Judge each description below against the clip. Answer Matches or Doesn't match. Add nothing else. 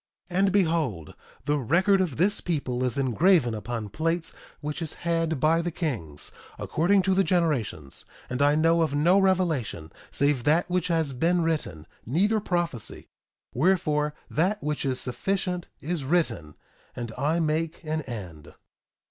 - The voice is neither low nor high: Matches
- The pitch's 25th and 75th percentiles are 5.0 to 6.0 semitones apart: Matches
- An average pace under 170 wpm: Matches